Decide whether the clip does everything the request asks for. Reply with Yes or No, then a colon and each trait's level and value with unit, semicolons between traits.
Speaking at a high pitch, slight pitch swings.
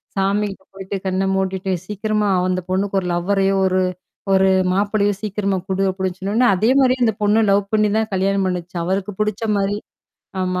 Yes: high, 195 Hz; narrow, 1.8 semitones